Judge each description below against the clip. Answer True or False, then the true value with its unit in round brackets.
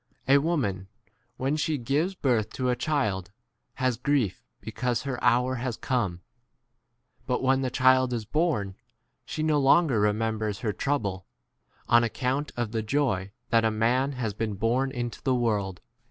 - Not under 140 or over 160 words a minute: False (170 wpm)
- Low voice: True (125 Hz)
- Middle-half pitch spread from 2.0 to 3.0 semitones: False (3.8 semitones)